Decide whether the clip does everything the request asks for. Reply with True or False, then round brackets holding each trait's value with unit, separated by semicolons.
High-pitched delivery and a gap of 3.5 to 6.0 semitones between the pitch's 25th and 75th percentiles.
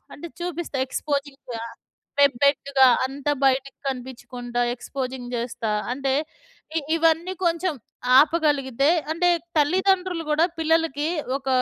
True (280 Hz; 3.8 semitones)